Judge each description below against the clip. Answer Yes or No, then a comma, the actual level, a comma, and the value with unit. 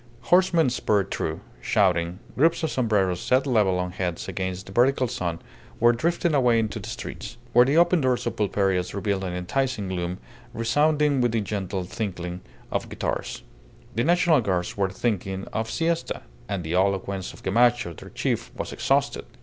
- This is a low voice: Yes, low, 105 Hz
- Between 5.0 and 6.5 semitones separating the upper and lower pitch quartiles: Yes, wide, 5.5 semitones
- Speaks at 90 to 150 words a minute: No, average, 165 wpm